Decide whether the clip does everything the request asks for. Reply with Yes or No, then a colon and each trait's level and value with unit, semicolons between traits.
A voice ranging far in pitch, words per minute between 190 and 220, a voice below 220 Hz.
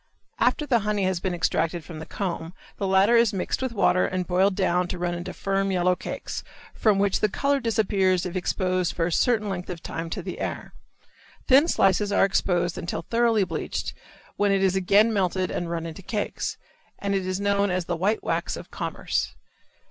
No: narrow, 2.4 semitones; average, 200 wpm; high, 190 Hz